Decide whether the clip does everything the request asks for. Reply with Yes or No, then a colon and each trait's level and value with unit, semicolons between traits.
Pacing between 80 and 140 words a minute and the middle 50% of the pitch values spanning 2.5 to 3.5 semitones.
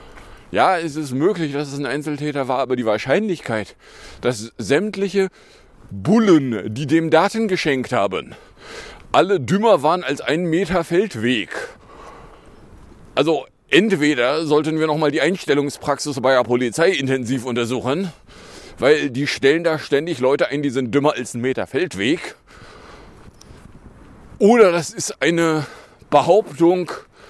No: average, 130 wpm; average, 4.1 semitones